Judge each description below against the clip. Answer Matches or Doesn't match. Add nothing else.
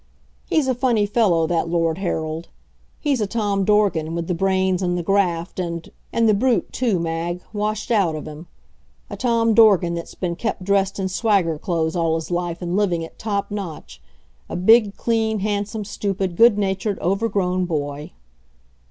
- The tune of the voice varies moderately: Matches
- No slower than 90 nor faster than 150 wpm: Doesn't match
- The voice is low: Doesn't match